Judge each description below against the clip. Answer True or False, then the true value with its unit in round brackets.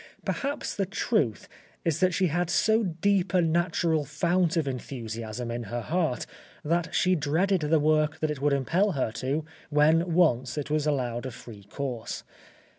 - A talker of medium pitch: True (155 Hz)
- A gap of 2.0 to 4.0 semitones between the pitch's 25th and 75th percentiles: False (5.0 semitones)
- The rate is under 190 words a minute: True (170 wpm)